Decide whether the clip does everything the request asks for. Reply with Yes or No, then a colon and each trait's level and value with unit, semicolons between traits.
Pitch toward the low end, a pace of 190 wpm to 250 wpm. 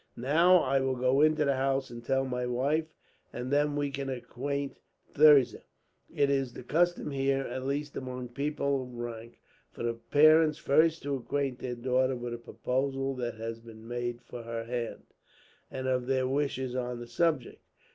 No: low, 130 Hz; average, 175 wpm